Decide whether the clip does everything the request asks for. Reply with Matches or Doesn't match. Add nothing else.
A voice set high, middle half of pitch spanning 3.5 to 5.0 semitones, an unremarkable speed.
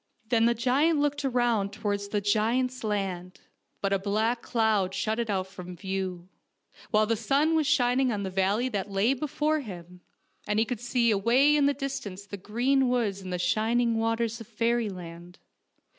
Matches